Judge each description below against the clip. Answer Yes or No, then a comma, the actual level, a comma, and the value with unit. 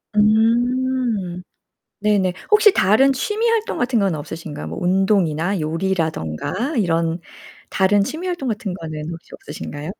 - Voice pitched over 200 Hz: No, high, 195 Hz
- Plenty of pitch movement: Yes, wide, 6.9 semitones